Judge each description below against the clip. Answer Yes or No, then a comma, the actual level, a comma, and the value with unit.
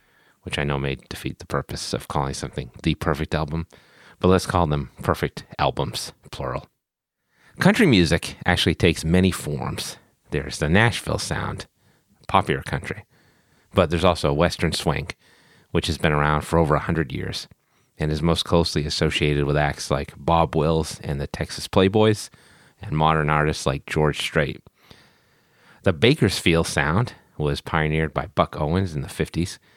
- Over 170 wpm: No, average, 155 wpm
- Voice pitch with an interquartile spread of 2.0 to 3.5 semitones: Yes, average, 2.7 semitones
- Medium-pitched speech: No, very low, 80 Hz